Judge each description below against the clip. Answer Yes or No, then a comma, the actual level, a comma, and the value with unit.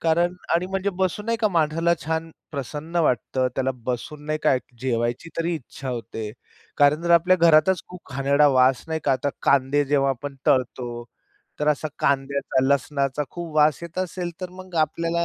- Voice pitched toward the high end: No, medium, 150 Hz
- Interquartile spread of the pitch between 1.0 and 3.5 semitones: No, average, 3.9 semitones